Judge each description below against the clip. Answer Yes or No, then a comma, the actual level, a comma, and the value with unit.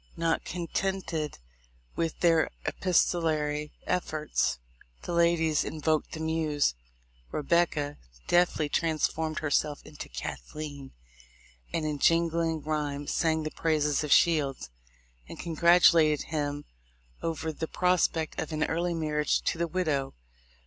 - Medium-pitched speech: Yes, medium, 155 Hz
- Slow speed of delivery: Yes, slow, 115 wpm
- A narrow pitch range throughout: Yes, narrow, 1.9 semitones